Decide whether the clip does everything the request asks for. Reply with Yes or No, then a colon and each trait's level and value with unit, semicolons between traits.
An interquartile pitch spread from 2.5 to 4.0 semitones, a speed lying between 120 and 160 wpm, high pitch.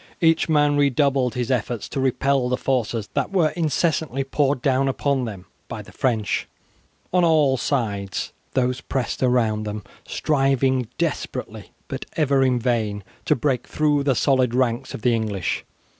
No: average, 3.0 semitones; average, 155 wpm; low, 130 Hz